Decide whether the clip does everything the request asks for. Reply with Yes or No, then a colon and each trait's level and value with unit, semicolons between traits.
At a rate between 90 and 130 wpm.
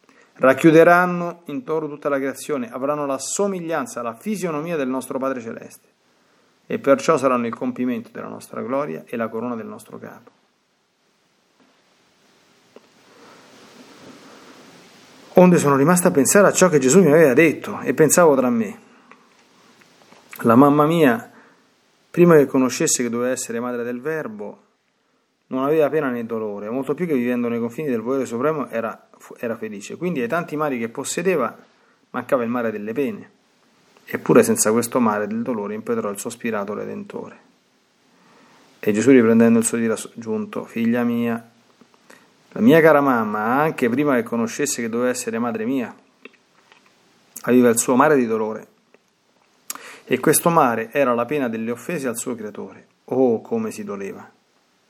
No: average, 150 wpm